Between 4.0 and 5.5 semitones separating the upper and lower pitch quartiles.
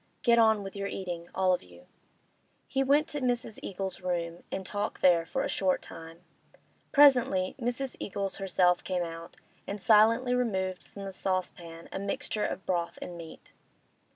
Yes: average, 4.3 semitones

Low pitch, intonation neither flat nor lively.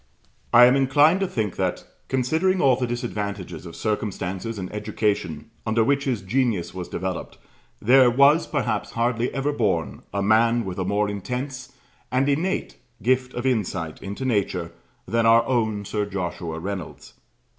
Yes: low, 115 Hz; average, 4.5 semitones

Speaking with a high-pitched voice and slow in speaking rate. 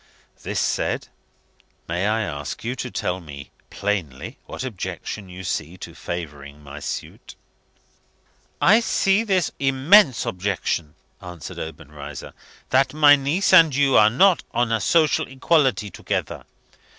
No: low, 110 Hz; slow, 130 wpm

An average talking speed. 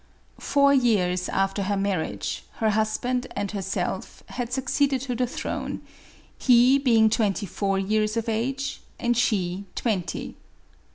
No: slow, 130 wpm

